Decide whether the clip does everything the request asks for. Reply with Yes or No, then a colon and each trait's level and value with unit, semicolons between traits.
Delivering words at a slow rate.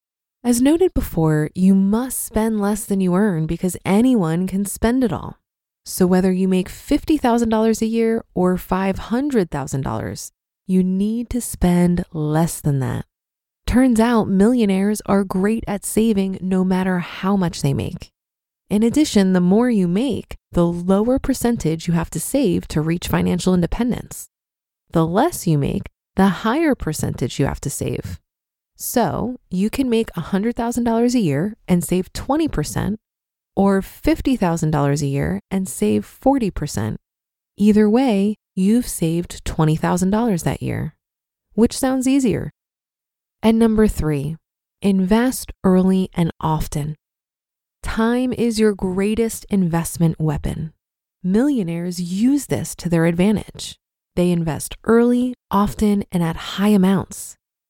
Yes: slow, 130 wpm